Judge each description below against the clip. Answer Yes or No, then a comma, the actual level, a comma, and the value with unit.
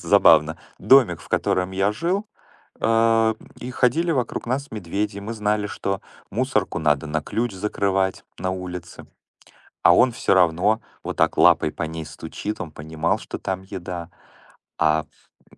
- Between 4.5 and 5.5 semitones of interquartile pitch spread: Yes, average, 5.2 semitones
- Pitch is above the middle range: No, very low, 95 Hz